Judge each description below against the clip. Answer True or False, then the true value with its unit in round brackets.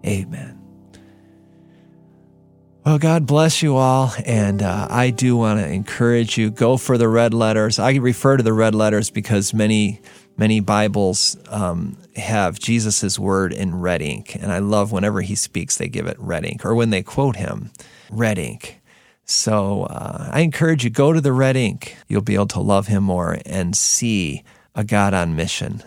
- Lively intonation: False (3.7 semitones)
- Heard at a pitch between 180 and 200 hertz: False (105 Hz)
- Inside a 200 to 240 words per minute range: False (180 wpm)